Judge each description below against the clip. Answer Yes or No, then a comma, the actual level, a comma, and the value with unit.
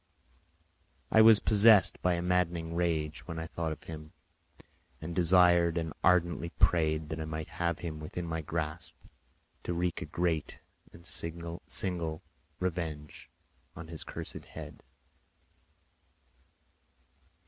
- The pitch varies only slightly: Yes, narrow, 1.8 semitones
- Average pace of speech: No, slow, 125 wpm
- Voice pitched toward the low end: Yes, very low, 85 Hz